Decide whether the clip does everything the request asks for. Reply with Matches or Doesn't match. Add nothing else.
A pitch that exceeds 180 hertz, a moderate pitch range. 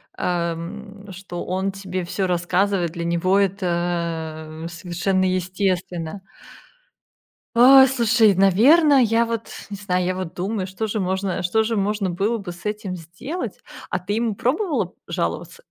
Matches